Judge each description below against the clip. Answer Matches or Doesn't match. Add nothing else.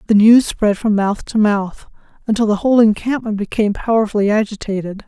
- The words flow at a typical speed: Matches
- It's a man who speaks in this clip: Doesn't match